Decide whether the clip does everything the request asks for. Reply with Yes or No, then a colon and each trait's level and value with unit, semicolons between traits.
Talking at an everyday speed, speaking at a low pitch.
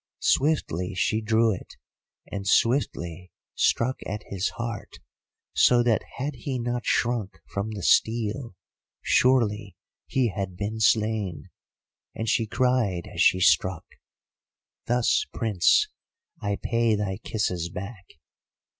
No: slow, 120 wpm; low, 110 Hz